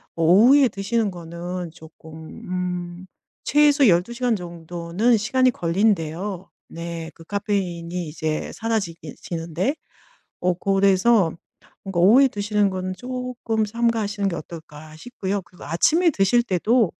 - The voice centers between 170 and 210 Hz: Yes, high, 190 Hz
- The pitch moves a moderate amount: Yes, average, 4.8 semitones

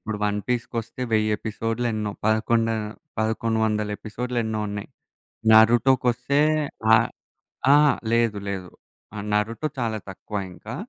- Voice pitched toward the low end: Yes, low, 110 Hz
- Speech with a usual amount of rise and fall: No, narrow, 1.9 semitones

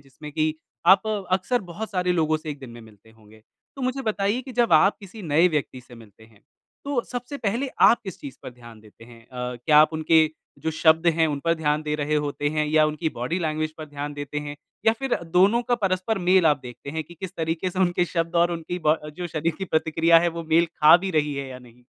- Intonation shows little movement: No, average, 4.1 semitones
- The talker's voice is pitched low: No, medium, 160 Hz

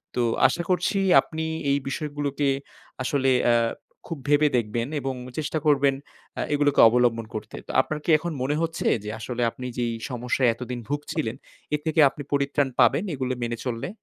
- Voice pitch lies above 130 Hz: Yes, medium, 140 Hz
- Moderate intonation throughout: Yes, average, 3.4 semitones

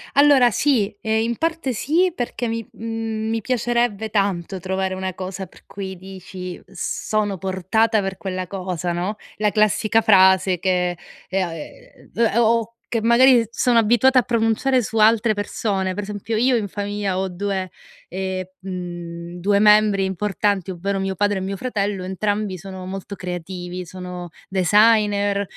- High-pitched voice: Yes, high, 200 Hz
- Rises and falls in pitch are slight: No, average, 3.0 semitones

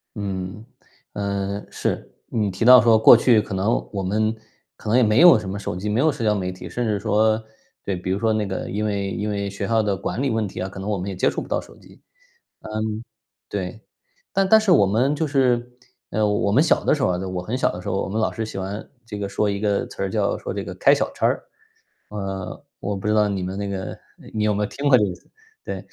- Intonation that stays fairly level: Yes, narrow, 2.3 semitones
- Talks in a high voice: No, low, 105 Hz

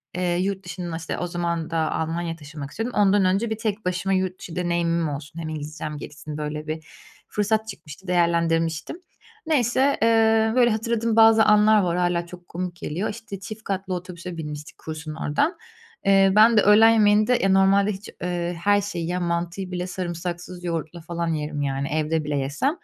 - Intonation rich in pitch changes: No, average, 4.0 semitones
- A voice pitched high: No, medium, 180 Hz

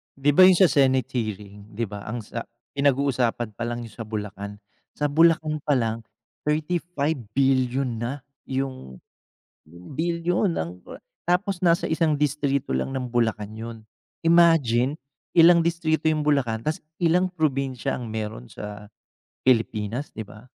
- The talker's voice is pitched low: Yes, low, 130 Hz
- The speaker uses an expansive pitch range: Yes, wide, 5.9 semitones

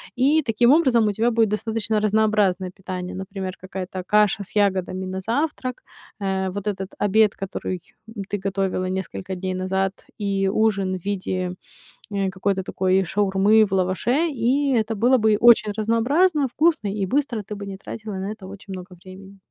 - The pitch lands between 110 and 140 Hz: No, high, 200 Hz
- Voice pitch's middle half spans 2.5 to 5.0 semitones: Yes, average, 2.8 semitones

